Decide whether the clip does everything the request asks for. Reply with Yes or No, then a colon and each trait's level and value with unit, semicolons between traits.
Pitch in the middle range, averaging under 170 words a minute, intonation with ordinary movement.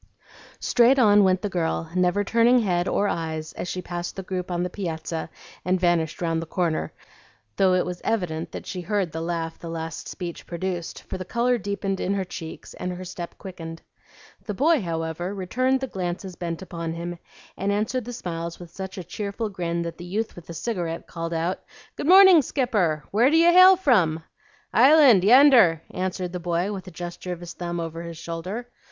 No: medium, 180 Hz; average, 195 wpm; average, 3.5 semitones